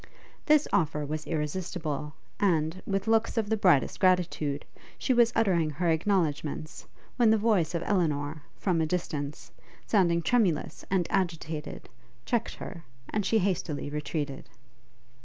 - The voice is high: No, medium, 170 Hz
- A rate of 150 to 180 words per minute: No, slow, 135 wpm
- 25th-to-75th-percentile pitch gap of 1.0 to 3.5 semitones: No, average, 4.7 semitones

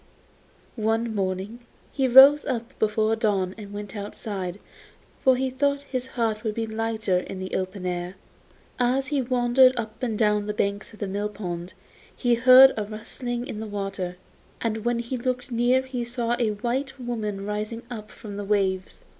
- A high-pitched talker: Yes, high, 220 Hz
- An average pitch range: Yes, average, 3.2 semitones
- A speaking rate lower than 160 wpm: No, average, 180 wpm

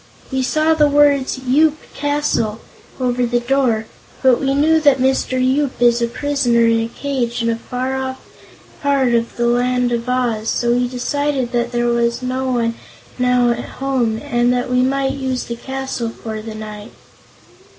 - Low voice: No, very high, 250 Hz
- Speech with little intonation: Yes, narrow, 2.1 semitones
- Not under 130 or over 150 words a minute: No, average, 170 wpm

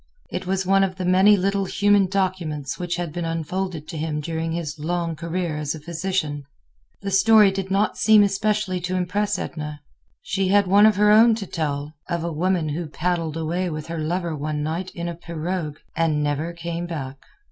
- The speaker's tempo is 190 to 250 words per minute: Yes, average, 195 wpm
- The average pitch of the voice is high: No, medium, 175 Hz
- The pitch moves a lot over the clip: No, average, 3.4 semitones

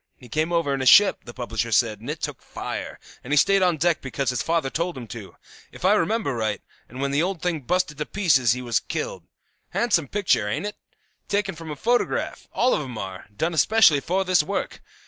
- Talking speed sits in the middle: No, fast, 225 wpm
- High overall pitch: No, medium, 155 Hz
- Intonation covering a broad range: Yes, wide, 6.4 semitones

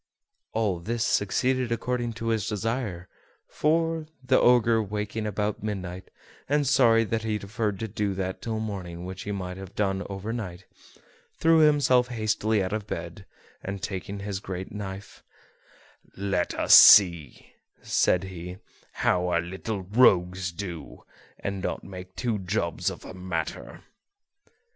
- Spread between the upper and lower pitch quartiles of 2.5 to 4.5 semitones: Yes, average, 3.4 semitones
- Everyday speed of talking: Yes, average, 145 wpm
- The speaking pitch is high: No, low, 100 Hz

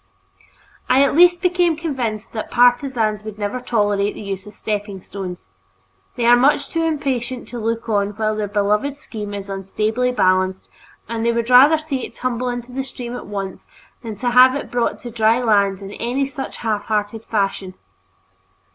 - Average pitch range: Yes, average, 3.7 semitones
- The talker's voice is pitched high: Yes, high, 230 Hz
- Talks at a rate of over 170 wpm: Yes, average, 180 wpm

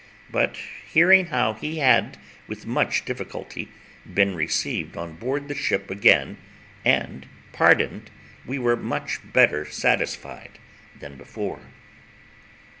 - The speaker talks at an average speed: No, slow, 115 wpm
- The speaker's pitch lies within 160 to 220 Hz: No, low, 120 Hz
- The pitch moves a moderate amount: No, wide, 8.9 semitones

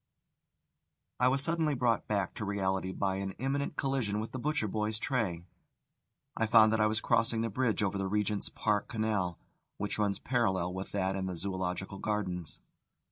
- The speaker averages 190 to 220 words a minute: No, average, 175 wpm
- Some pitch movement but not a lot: Yes, average, 3.2 semitones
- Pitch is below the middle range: Yes, low, 105 Hz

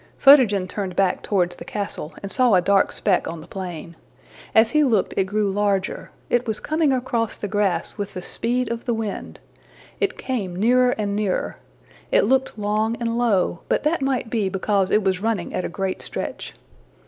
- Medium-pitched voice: No, high, 210 Hz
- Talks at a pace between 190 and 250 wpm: Yes, average, 195 wpm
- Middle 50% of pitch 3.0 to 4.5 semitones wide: Yes, average, 3.9 semitones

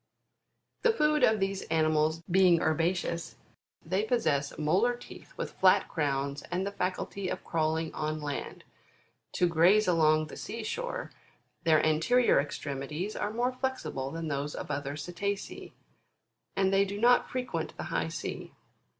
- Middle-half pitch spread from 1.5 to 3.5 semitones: No, average, 5.0 semitones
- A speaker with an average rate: Yes, average, 150 wpm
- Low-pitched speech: No, medium, 170 Hz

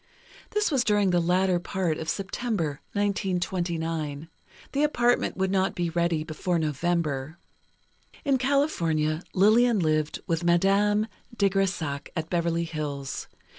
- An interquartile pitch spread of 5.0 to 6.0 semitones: No, average, 4.0 semitones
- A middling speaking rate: No, slow, 125 wpm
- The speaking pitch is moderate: Yes, medium, 175 Hz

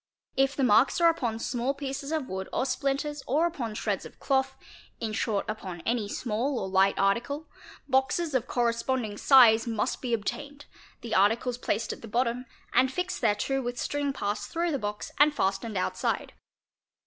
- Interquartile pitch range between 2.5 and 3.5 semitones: No, average, 4.2 semitones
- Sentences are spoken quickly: No, average, 180 wpm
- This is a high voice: Yes, high, 245 Hz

